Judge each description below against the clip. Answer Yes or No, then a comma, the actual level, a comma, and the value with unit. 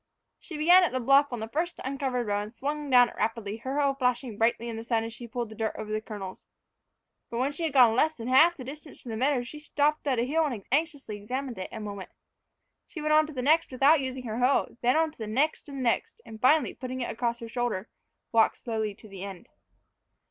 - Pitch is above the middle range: Yes, very high, 250 Hz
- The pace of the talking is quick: Yes, fast, 250 wpm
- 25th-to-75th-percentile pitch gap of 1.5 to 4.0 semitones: No, average, 4.4 semitones